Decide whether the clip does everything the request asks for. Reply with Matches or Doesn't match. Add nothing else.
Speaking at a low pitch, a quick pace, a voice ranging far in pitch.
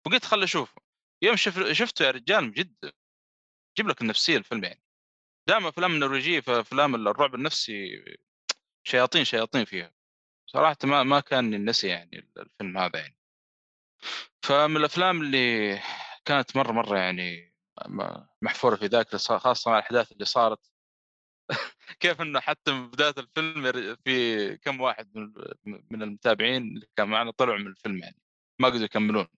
Matches